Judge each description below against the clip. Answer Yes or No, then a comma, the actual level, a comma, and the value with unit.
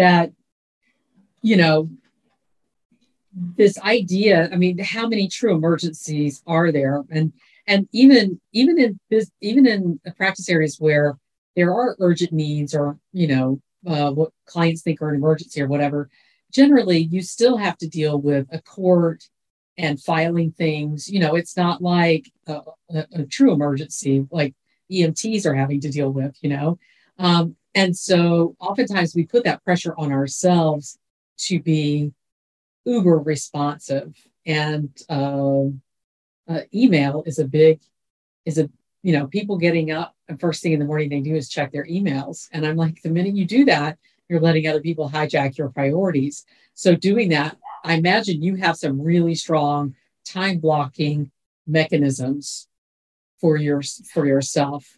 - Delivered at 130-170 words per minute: Yes, average, 155 wpm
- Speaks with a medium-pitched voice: Yes, medium, 160 Hz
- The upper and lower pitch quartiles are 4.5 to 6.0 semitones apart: No, average, 3.7 semitones